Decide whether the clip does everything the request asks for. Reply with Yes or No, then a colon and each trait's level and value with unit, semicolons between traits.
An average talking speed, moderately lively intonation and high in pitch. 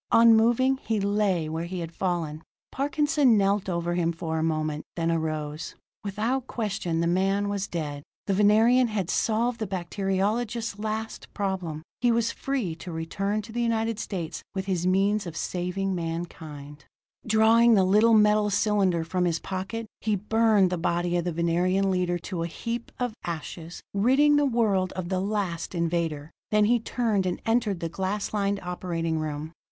Yes: average, 170 wpm; average, 4.4 semitones; high, 195 Hz